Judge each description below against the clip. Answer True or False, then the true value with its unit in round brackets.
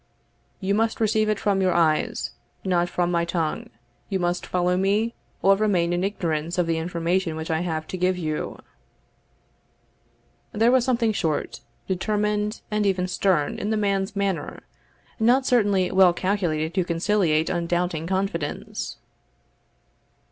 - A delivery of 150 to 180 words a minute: False (140 wpm)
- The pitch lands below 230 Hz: True (185 Hz)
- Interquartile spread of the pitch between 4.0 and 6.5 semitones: False (3.3 semitones)